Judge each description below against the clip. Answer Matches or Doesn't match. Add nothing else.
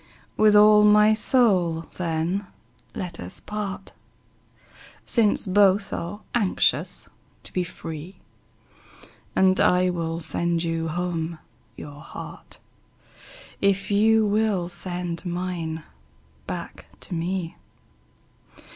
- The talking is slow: Matches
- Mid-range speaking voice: Matches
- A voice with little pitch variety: Doesn't match